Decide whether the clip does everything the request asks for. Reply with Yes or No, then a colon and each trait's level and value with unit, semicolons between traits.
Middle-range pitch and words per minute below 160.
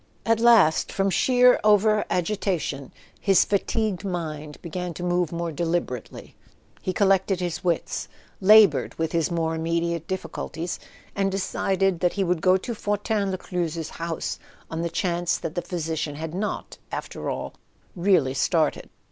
Yes: medium, 175 Hz; average, 145 wpm